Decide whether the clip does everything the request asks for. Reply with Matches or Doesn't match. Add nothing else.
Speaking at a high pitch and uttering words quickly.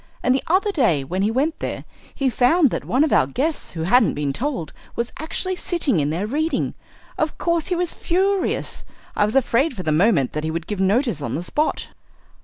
Matches